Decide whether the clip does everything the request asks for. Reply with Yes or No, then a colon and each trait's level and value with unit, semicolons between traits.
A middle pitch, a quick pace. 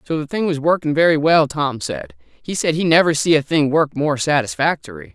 Yes: medium, 155 Hz; fast, 220 wpm